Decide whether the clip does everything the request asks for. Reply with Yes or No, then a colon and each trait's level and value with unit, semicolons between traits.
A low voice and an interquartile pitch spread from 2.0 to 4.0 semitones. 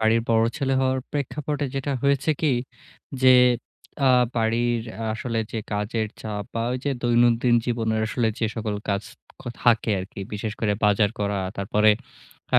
Yes: low, 115 Hz; average, 3.1 semitones